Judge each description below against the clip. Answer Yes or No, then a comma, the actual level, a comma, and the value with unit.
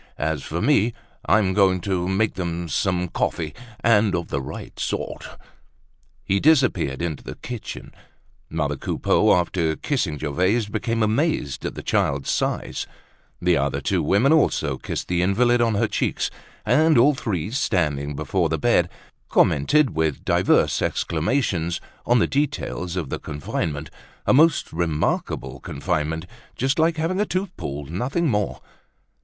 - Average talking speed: Yes, average, 145 wpm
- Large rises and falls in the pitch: Yes, wide, 7.2 semitones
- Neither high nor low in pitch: No, very low, 95 Hz